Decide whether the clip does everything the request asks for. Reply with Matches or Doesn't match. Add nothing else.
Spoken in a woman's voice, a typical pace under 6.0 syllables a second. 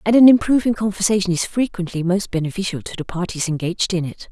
Doesn't match